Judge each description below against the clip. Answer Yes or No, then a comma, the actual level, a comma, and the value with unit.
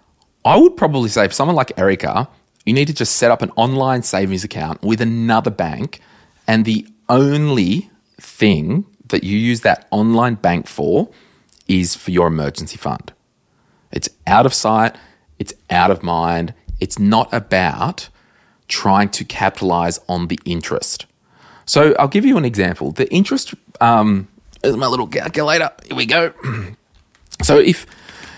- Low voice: Yes, low, 110 Hz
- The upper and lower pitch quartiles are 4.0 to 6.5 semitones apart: Yes, average, 4.6 semitones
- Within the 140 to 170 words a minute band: Yes, average, 150 wpm